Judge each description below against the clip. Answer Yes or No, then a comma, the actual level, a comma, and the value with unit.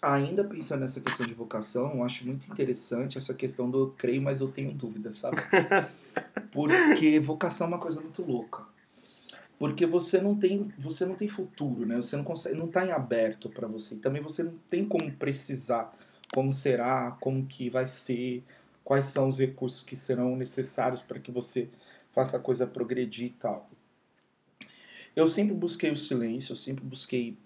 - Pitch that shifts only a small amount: No, average, 3.9 semitones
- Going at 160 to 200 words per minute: Yes, average, 175 wpm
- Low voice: Yes, low, 130 Hz